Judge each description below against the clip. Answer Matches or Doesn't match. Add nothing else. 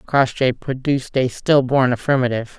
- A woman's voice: Matches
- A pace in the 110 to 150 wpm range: Matches